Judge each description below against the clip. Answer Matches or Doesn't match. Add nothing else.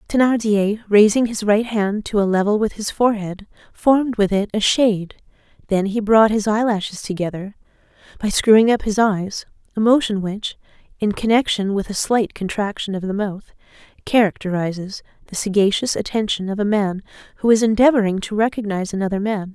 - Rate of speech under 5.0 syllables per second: Doesn't match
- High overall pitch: Matches